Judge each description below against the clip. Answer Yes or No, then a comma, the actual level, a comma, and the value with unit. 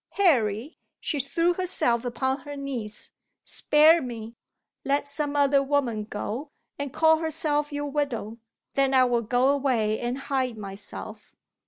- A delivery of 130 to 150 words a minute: Yes, average, 140 wpm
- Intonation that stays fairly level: No, average, 3.7 semitones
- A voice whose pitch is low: No, very high, 275 Hz